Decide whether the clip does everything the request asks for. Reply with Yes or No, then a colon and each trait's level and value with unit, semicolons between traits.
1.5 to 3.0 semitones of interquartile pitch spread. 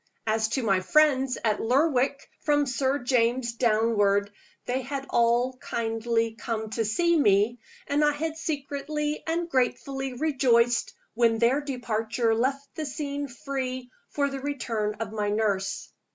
No: average, 3.8 semitones